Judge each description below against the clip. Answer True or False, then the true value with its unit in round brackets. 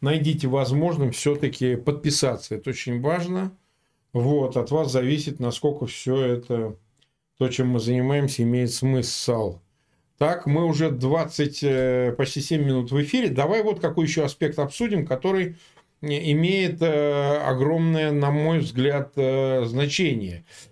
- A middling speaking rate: True (120 wpm)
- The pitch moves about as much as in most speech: True (3.5 semitones)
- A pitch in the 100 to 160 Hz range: True (140 Hz)